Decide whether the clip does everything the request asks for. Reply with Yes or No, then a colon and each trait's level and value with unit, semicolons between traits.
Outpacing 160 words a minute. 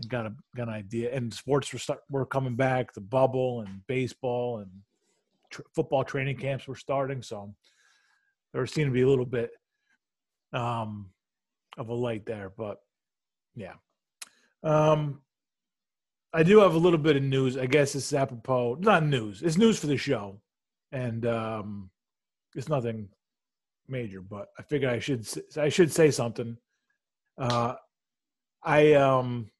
No: average, 155 wpm